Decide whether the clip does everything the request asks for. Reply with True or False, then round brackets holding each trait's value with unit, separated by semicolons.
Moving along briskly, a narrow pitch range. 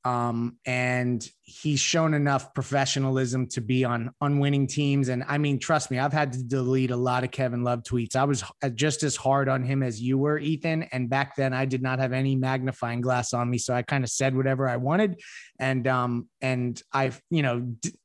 True (215 wpm; 1.9 semitones)